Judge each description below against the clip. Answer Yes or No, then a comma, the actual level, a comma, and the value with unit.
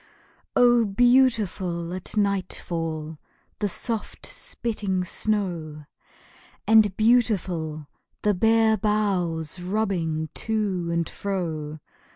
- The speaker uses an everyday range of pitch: Yes, average, 4.5 semitones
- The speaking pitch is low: No, high, 190 Hz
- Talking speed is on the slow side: Yes, slow, 85 wpm